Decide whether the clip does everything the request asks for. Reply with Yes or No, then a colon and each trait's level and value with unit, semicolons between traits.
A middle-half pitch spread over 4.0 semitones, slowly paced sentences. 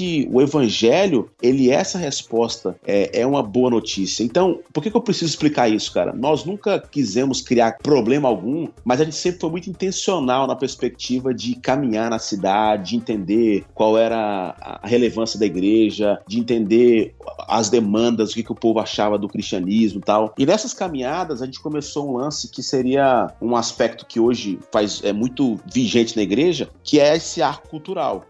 No: average, 5.0 semitones; average, 180 wpm